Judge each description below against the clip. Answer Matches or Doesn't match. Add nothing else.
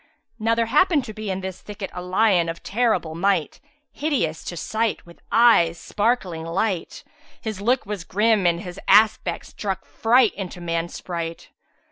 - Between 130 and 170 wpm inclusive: Matches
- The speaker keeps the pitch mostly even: Doesn't match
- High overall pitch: Matches